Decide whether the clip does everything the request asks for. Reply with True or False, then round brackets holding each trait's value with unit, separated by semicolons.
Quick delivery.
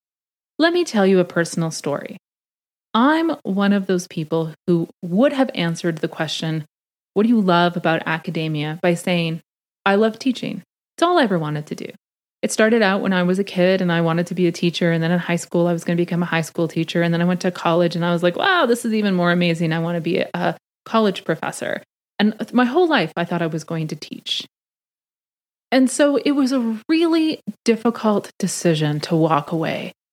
True (220 wpm)